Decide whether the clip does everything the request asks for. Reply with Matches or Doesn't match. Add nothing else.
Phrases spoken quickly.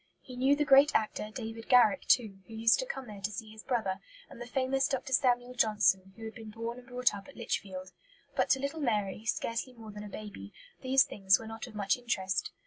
Matches